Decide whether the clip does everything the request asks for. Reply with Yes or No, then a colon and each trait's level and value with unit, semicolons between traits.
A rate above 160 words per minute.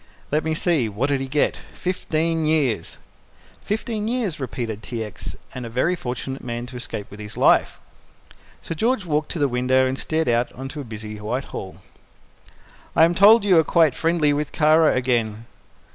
Yes: average, 175 wpm